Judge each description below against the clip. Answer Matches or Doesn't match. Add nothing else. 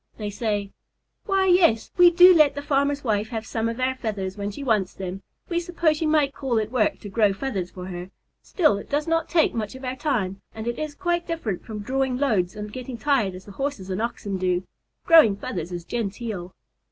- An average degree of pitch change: Doesn't match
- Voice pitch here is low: Doesn't match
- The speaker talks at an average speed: Doesn't match